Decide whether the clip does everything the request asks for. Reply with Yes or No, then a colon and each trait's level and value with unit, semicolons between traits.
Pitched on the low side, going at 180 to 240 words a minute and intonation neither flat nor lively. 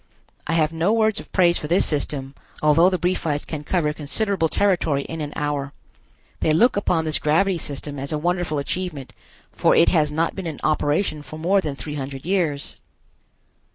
No: medium, 155 Hz; average, 185 wpm; average, 3.4 semitones